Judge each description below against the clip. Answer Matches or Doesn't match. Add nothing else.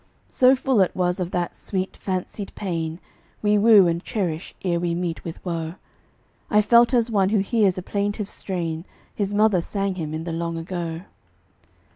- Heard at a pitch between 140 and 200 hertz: Matches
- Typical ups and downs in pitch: Matches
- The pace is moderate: Matches